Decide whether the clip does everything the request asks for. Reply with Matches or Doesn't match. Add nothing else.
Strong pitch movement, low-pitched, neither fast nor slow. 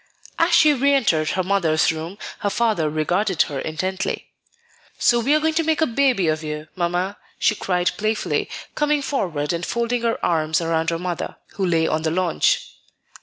Doesn't match